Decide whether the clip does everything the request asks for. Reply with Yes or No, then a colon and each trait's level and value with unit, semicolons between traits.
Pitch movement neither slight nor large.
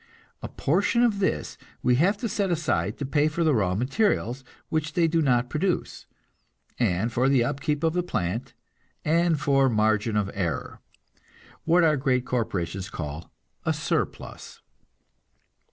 No: wide, 7.1 semitones